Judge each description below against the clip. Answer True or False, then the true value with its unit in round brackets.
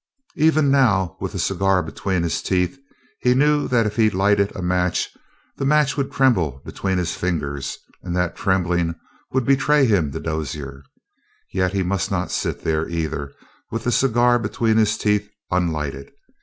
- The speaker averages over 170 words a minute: False (165 wpm)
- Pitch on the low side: True (95 Hz)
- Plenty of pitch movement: True (6.1 semitones)